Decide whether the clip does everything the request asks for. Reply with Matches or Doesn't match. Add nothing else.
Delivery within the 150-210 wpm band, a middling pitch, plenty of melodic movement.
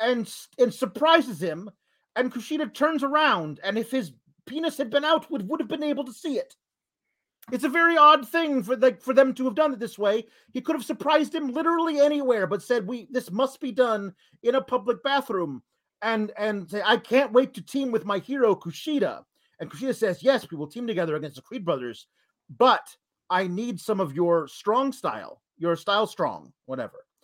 Doesn't match